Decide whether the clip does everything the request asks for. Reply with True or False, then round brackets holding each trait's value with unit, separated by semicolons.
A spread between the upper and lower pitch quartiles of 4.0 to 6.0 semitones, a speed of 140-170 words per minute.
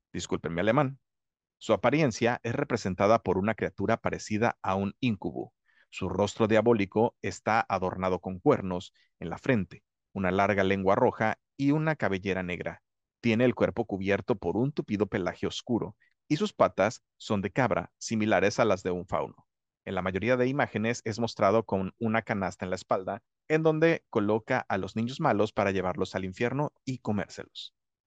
True (4.3 semitones; 165 wpm)